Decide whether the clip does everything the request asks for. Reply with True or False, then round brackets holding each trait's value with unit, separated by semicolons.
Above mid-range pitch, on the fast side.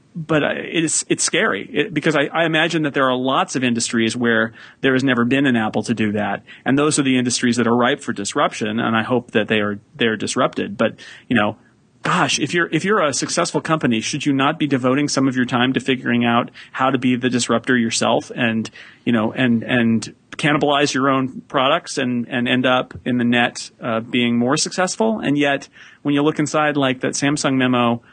False (130 Hz; 220 wpm)